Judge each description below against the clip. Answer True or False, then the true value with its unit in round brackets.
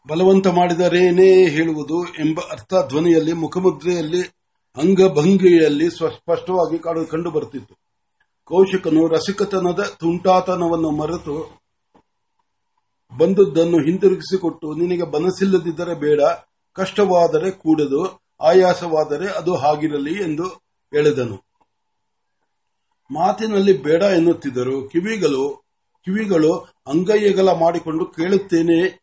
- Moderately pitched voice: True (175 Hz)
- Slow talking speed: True (70 wpm)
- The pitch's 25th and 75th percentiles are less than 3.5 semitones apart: True (2.9 semitones)